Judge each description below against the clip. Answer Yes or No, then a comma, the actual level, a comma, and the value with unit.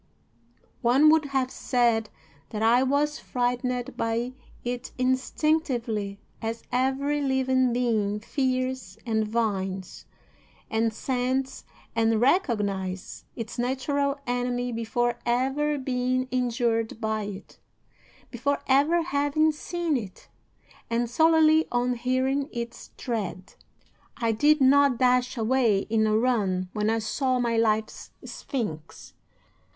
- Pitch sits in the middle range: No, high, 245 Hz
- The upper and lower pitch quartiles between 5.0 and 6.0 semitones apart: No, average, 3.0 semitones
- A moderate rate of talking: No, slow, 115 wpm